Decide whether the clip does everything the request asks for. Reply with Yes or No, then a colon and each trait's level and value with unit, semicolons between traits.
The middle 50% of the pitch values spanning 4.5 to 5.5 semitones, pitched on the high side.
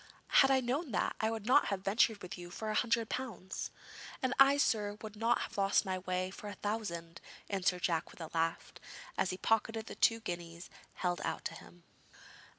No: average, 4.1 semitones; high, 205 Hz